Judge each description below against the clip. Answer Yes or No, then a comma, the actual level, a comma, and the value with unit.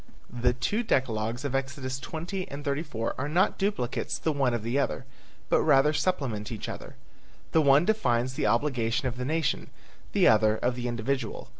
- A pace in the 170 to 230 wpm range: Yes, average, 175 wpm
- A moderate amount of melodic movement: Yes, average, 3.7 semitones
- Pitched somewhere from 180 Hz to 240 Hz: No, low, 130 Hz